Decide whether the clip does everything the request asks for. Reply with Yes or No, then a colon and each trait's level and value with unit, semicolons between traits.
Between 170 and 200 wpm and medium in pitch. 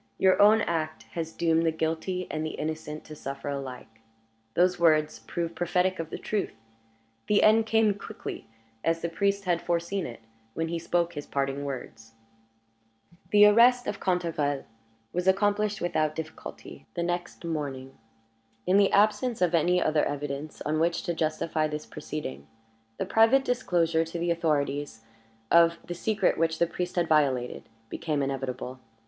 No: average, 155 wpm; medium, 165 Hz